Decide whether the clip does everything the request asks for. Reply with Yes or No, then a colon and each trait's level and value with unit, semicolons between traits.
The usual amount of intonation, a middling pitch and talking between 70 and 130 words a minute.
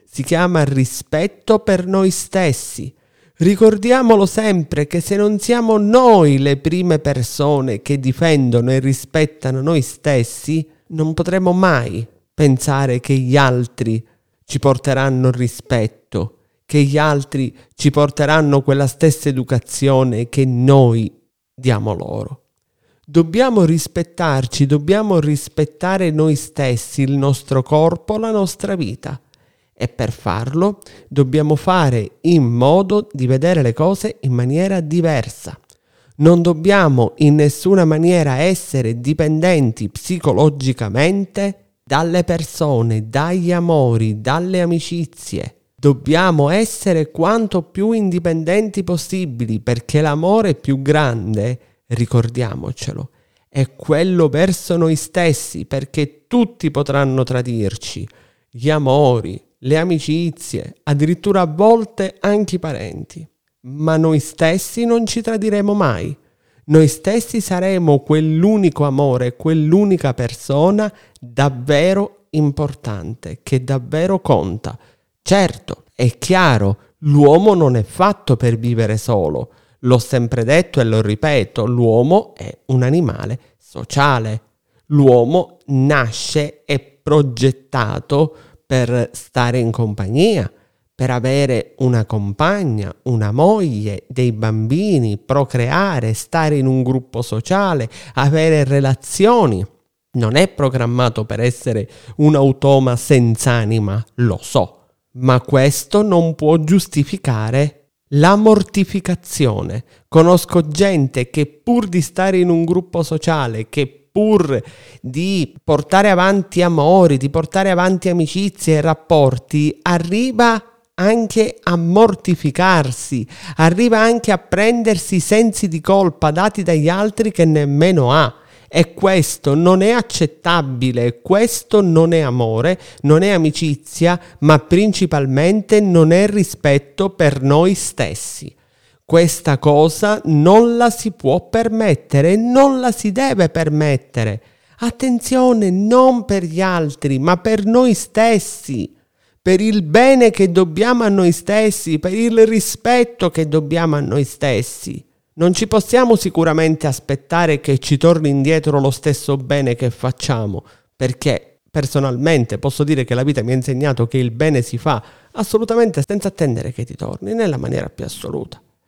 No: wide, 6.0 semitones; medium, 150 Hz; average, 120 wpm